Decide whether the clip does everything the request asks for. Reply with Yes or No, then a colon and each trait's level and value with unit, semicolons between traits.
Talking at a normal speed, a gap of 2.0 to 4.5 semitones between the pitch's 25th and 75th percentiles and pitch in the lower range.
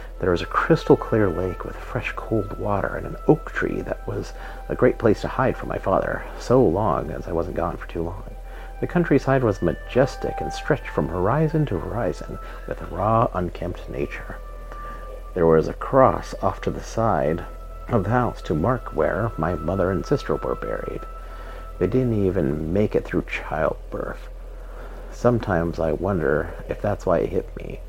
No: average, 180 wpm; average, 5.2 semitones; very low, 95 Hz